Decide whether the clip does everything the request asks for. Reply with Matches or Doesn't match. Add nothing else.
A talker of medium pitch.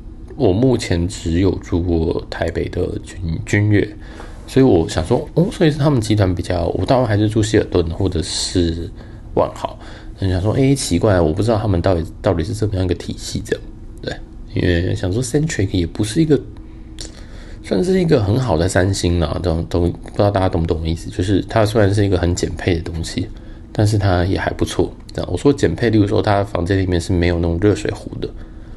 Doesn't match